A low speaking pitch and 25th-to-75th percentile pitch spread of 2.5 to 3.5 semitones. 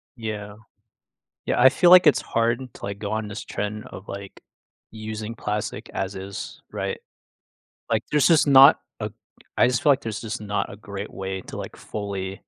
Yes: low, 105 Hz; average, 2.8 semitones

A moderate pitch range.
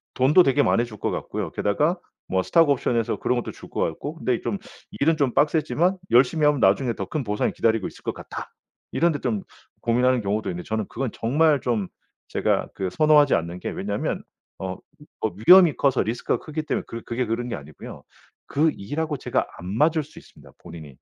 No: wide, 6.2 semitones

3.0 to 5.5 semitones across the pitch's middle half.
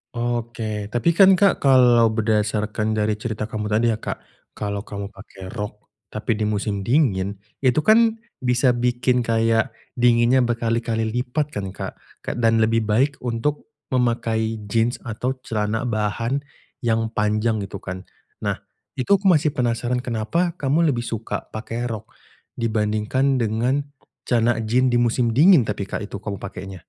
No: narrow, 2.5 semitones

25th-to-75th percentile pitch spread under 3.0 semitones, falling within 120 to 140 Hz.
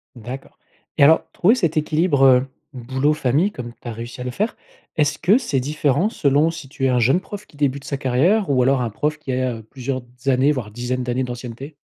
No: average, 3.3 semitones; low, 135 Hz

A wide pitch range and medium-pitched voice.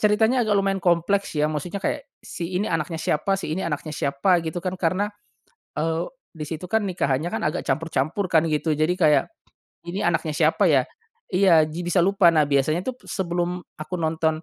No: average, 3.6 semitones; medium, 170 Hz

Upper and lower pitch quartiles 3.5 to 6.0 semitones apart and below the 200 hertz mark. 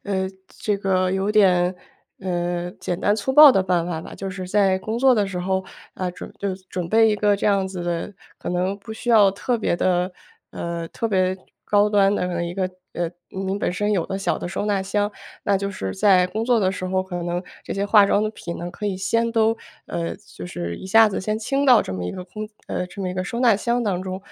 No: narrow, 2.6 semitones; high, 190 Hz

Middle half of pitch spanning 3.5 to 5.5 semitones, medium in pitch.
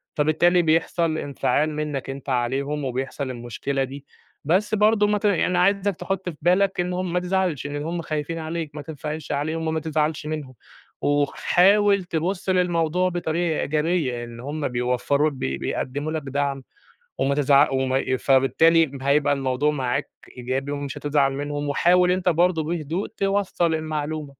Yes: average, 3.9 semitones; medium, 155 Hz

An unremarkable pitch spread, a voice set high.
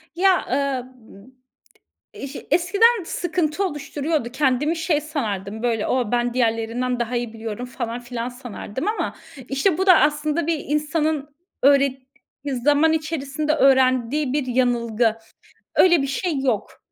Yes: average, 4.1 semitones; very high, 275 Hz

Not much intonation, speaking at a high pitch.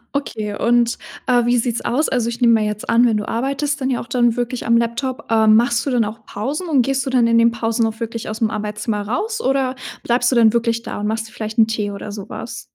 Yes: narrow, 2.2 semitones; high, 235 Hz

